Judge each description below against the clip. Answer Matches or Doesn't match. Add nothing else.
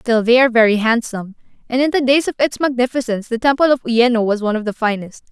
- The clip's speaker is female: Matches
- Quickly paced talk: Matches